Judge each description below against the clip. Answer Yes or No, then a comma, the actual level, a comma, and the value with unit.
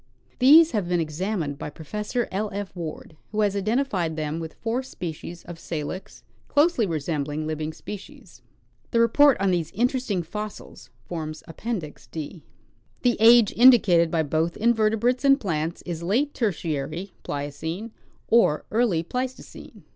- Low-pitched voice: No, high, 190 Hz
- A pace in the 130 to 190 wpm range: Yes, average, 145 wpm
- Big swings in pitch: Yes, wide, 6.4 semitones